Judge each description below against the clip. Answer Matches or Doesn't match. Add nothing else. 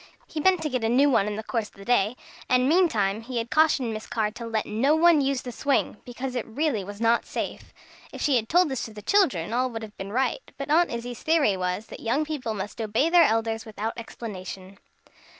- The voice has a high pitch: Matches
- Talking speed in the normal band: Doesn't match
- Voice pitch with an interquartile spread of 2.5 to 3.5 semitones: Doesn't match